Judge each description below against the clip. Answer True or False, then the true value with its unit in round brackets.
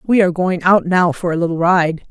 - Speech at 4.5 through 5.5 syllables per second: True (5.4 syllables/s)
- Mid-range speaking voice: True (175 Hz)